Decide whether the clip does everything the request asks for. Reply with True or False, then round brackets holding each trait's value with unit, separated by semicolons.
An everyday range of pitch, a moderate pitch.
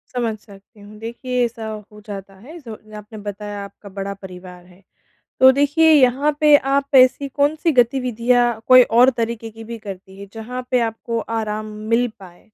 False (3.8 semitones; 225 Hz)